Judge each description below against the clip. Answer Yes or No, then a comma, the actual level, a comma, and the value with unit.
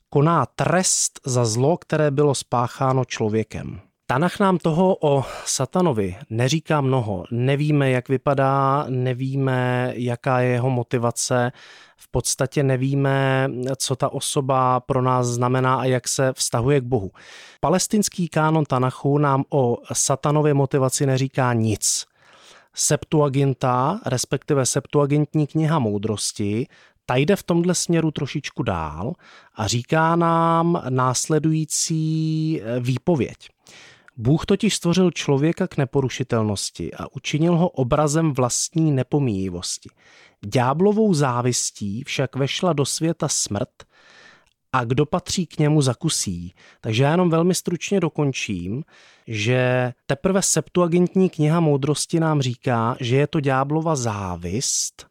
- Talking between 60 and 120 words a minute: Yes, slow, 115 wpm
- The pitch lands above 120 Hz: Yes, medium, 140 Hz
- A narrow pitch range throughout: No, average, 4.0 semitones